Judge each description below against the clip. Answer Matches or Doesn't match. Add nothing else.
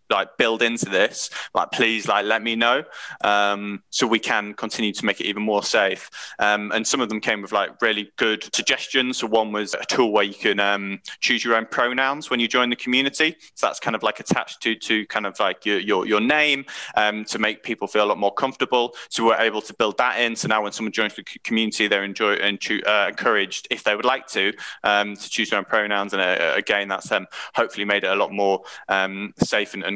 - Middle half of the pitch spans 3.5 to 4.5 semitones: Doesn't match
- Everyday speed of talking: Doesn't match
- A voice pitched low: Matches